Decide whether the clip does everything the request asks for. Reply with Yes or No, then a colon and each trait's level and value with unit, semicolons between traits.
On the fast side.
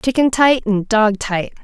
No: average, 185 wpm